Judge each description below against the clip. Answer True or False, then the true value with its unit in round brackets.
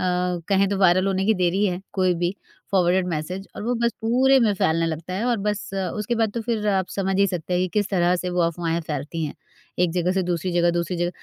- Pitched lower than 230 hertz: True (185 Hz)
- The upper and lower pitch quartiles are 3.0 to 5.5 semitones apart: False (2.4 semitones)